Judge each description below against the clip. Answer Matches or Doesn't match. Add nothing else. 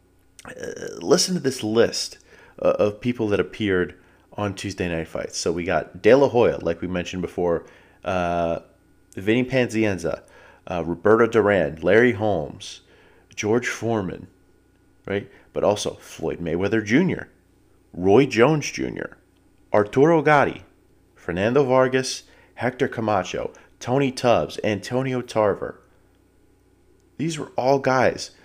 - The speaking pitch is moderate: Doesn't match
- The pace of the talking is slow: Matches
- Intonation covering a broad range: Matches